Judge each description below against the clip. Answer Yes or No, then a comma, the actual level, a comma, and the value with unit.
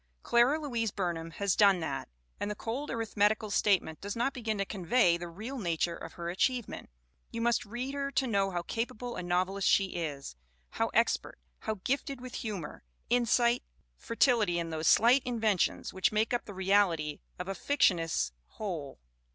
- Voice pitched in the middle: No, high, 205 Hz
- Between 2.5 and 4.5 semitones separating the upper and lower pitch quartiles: No, average, 5.3 semitones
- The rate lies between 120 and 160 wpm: No, average, 170 wpm